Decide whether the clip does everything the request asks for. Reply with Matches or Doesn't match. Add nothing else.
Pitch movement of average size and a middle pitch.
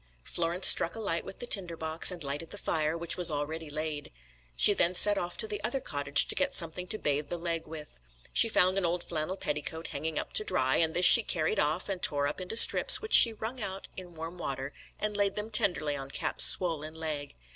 Matches